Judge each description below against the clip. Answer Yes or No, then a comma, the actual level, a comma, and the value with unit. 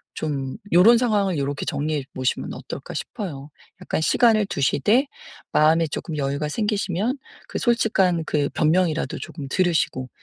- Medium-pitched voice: Yes, medium, 165 Hz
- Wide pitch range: Yes, wide, 6.2 semitones